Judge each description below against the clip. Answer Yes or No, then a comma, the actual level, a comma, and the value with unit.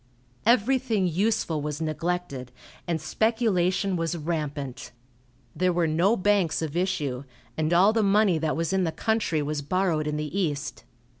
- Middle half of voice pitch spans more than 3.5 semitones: Yes, average, 4.2 semitones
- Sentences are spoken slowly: No, average, 150 wpm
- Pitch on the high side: No, medium, 170 Hz